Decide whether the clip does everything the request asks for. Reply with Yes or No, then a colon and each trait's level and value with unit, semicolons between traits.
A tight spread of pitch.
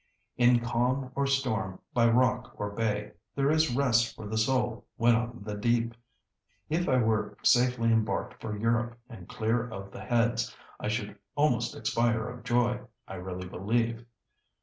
Yes: narrow, 2.1 semitones